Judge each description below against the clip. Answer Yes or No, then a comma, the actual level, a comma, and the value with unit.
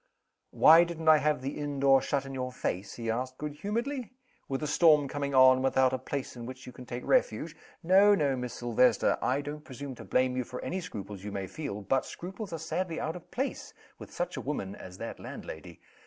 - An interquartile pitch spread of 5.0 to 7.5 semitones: No, average, 4.2 semitones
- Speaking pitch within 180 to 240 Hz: No, medium, 140 Hz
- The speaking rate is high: Yes, fast, 225 wpm